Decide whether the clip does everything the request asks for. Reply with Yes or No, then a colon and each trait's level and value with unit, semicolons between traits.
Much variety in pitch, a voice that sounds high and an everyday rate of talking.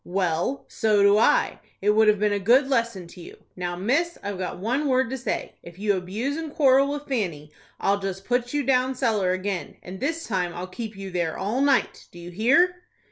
No: wide, 6.0 semitones; high, 215 Hz; fast, 215 wpm